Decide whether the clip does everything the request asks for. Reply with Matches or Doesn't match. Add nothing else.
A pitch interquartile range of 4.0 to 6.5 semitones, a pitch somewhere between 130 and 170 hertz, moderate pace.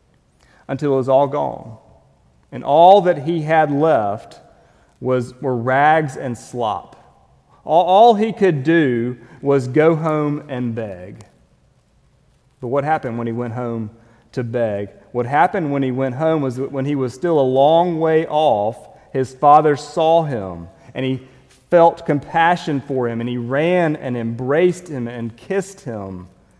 Matches